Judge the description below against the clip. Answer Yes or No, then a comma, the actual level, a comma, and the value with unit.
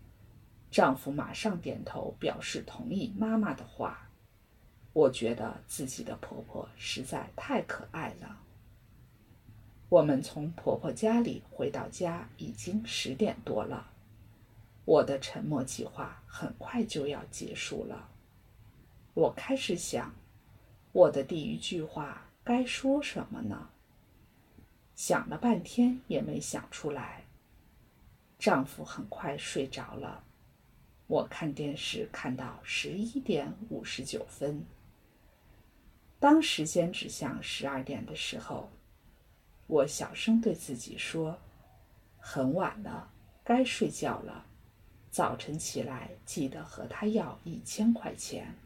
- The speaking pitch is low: No, medium, 160 Hz